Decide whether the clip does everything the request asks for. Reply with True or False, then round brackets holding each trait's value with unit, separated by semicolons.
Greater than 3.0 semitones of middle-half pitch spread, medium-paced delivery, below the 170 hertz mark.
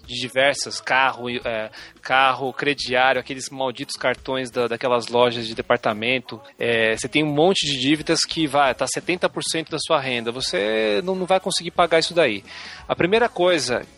True (4.8 semitones; 165 wpm; 135 Hz)